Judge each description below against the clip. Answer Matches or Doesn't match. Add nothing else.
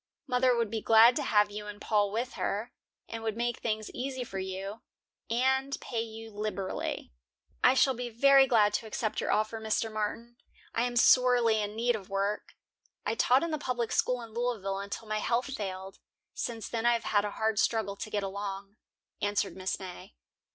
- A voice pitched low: Doesn't match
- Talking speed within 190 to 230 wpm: Matches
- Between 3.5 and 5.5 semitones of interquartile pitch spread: Doesn't match